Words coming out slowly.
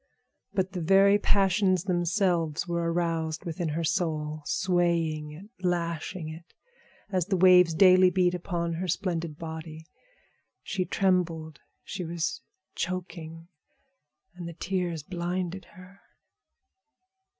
Yes: slow, 115 wpm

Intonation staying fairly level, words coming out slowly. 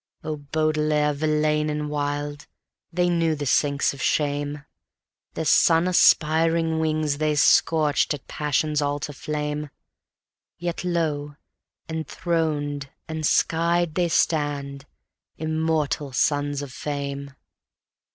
Yes: narrow, 1.8 semitones; slow, 105 wpm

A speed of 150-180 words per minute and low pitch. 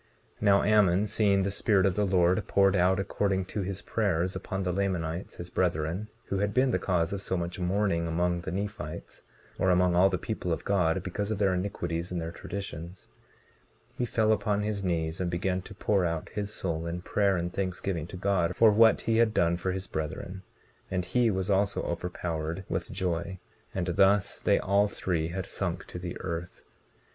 No: average, 195 wpm; very low, 95 Hz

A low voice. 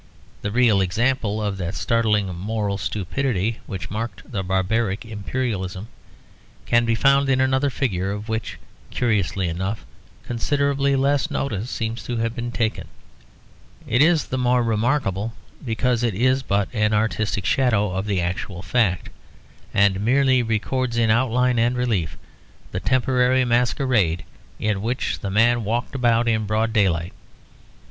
Yes: low, 115 Hz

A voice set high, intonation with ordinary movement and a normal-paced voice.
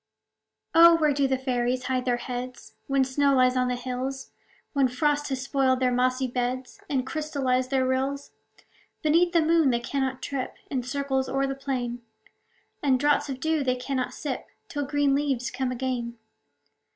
No: very high, 265 Hz; narrow, 1.9 semitones; average, 165 wpm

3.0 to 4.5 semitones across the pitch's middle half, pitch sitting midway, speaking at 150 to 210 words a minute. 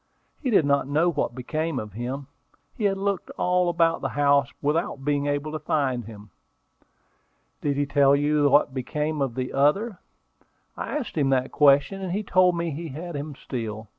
Yes: average, 3.7 semitones; medium, 145 Hz; average, 185 wpm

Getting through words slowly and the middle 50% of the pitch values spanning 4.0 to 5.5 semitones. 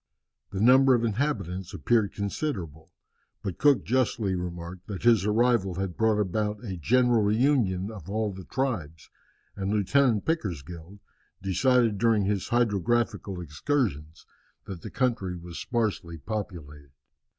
Yes: slow, 130 wpm; average, 4.8 semitones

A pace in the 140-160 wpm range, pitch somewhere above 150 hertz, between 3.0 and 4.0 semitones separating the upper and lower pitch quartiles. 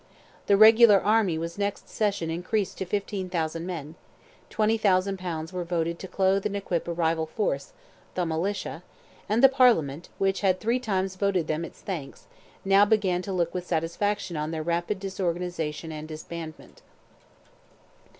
Yes: average, 145 wpm; medium, 185 Hz; average, 3.4 semitones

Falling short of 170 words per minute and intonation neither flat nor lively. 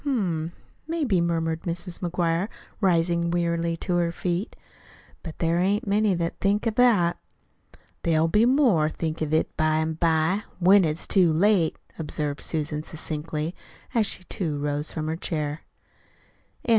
Yes: average, 150 wpm; average, 3.2 semitones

